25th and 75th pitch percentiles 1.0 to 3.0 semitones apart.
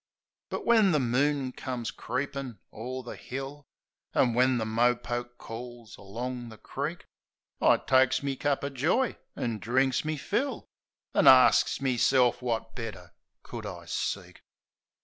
Yes: average, 2.7 semitones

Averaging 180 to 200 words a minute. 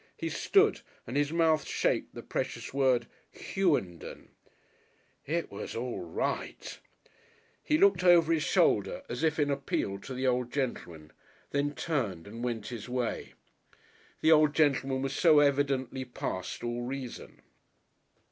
No: average, 140 wpm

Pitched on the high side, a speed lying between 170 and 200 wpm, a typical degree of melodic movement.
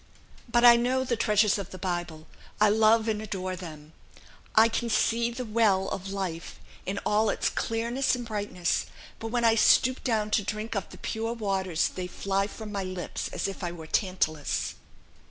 Yes: high, 210 Hz; average, 185 wpm; average, 3.5 semitones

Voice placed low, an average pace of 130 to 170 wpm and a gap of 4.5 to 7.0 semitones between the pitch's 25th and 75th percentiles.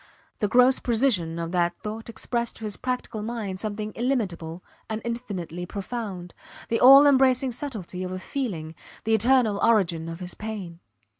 No: high, 215 Hz; average, 155 wpm; average, 5.1 semitones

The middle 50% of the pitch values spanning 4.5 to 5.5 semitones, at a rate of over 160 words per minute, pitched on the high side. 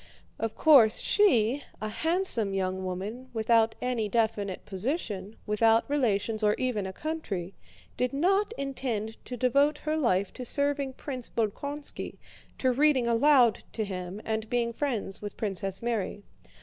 No: average, 5.0 semitones; average, 140 wpm; high, 230 Hz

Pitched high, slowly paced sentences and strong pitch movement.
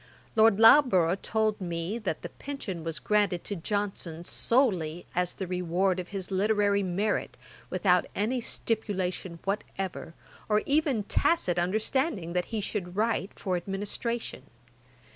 No: high, 195 Hz; slow, 130 wpm; average, 3.4 semitones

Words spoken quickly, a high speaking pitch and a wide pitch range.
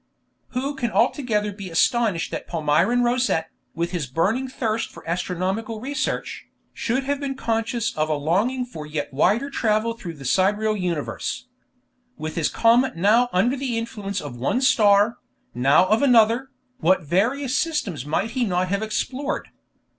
No: average, 155 wpm; high, 215 Hz; wide, 6.1 semitones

